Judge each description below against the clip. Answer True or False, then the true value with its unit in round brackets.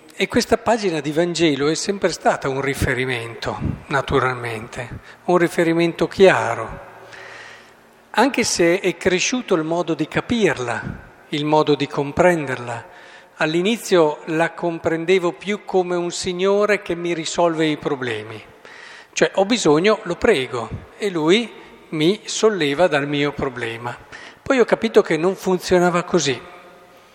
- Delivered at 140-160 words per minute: False (125 wpm)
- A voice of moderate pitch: True (170 Hz)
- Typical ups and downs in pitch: True (4.2 semitones)